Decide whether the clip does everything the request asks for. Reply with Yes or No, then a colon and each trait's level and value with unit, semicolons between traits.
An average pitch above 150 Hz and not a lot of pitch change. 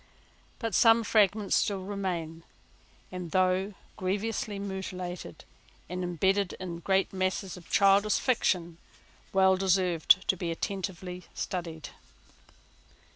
Yes: medium, 185 Hz; narrow, 1.9 semitones